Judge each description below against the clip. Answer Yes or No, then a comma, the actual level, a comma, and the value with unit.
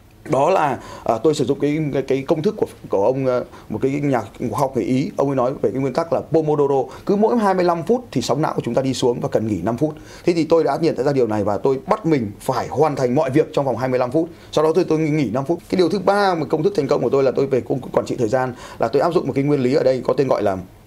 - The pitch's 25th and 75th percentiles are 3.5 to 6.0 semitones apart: Yes, average, 4.0 semitones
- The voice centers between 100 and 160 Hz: Yes, medium, 140 Hz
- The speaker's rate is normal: No, fast, 310 wpm